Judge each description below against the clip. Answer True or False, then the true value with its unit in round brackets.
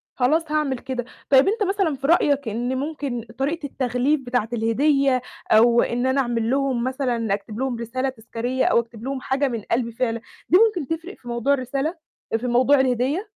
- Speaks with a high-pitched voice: True (260 Hz)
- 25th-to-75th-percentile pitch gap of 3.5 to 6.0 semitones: False (3.0 semitones)